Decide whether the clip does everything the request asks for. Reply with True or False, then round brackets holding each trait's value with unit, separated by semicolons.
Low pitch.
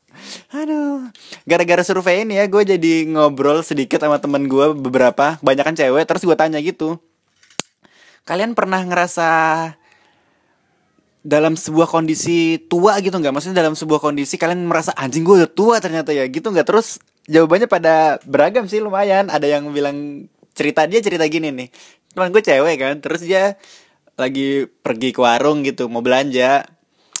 False (160 Hz)